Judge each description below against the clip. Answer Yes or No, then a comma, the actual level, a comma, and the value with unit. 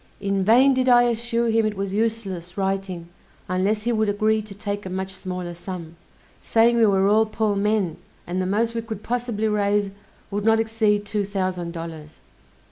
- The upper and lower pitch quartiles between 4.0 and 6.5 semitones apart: No, average, 2.8 semitones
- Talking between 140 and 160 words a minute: No, average, 185 wpm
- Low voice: No, high, 205 Hz